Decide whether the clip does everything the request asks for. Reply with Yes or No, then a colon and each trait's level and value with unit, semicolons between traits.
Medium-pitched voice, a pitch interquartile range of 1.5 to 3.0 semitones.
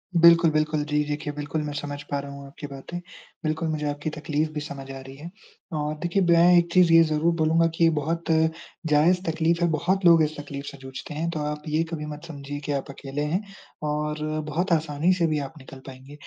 Yes: medium, 150 Hz; narrow, 2.4 semitones